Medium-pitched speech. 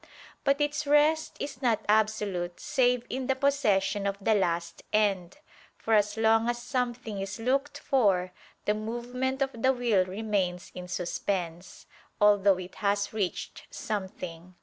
No: high, 215 Hz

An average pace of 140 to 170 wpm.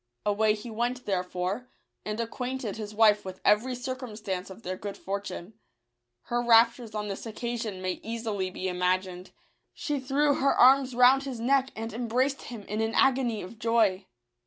Yes: average, 160 wpm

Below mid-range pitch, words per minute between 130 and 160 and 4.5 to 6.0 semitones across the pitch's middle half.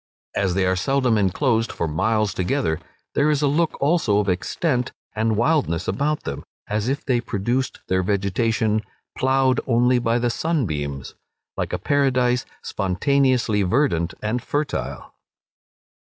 Yes: low, 115 Hz; average, 140 wpm; wide, 5.5 semitones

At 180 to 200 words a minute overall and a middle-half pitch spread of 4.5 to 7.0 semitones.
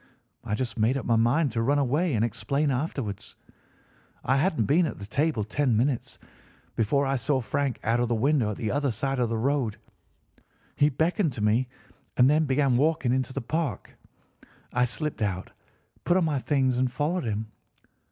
No: average, 185 wpm; average, 4.1 semitones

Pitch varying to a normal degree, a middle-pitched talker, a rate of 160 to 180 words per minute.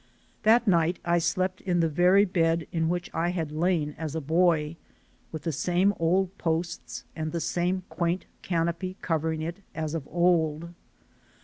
No: narrow, 1.9 semitones; medium, 170 Hz; average, 165 wpm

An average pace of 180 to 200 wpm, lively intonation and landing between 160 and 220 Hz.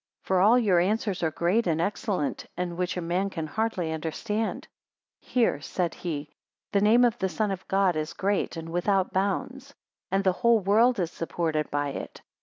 No: average, 190 wpm; average, 4.0 semitones; medium, 185 Hz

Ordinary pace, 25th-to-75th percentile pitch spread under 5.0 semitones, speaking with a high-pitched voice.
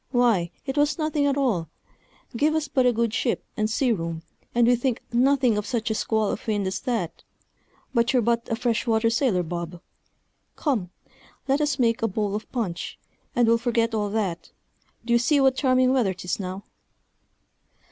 Yes: average, 185 wpm; average, 3.8 semitones; high, 235 Hz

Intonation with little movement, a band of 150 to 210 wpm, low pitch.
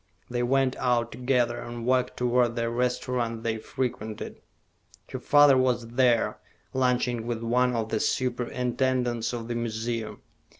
No: narrow, 1.4 semitones; slow, 135 wpm; low, 120 Hz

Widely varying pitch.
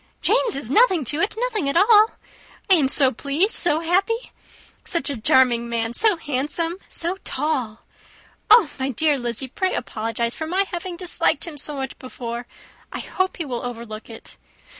Yes: wide, 6.9 semitones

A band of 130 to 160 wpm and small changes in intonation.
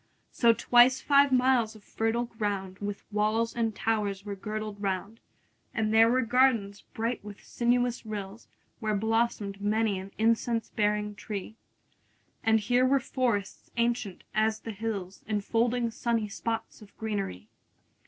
Yes: average, 145 wpm; narrow, 2.3 semitones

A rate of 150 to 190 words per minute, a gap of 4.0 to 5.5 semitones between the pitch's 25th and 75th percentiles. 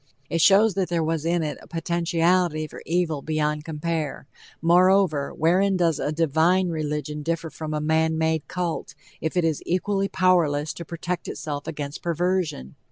No: average, 165 wpm; narrow, 2.6 semitones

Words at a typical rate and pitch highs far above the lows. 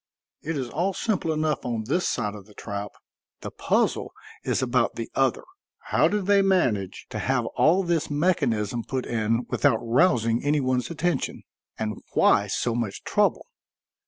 Yes: average, 160 wpm; wide, 6.4 semitones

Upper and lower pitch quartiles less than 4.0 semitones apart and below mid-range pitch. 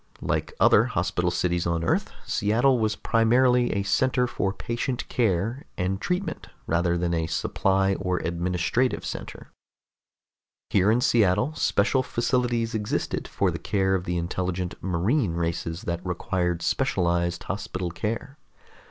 No: average, 5.2 semitones; very low, 95 Hz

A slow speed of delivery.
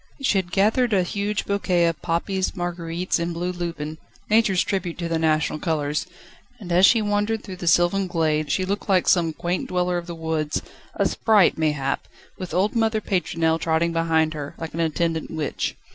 No: average, 185 wpm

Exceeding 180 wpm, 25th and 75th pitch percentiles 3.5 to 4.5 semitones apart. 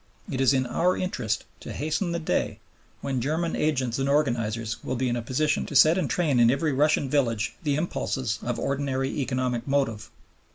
Yes: average, 190 wpm; average, 3.8 semitones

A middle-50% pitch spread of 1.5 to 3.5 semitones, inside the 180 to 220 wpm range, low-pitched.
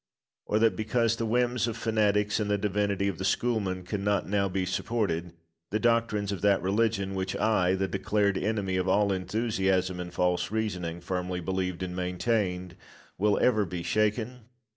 No: average, 2.8 semitones; average, 165 wpm; low, 100 Hz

